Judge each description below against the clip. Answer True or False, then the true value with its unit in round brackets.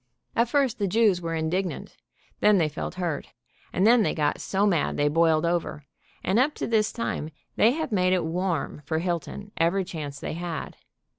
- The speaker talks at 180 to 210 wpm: True (190 wpm)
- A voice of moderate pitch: True (180 Hz)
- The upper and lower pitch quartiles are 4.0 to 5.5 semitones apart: True (4.5 semitones)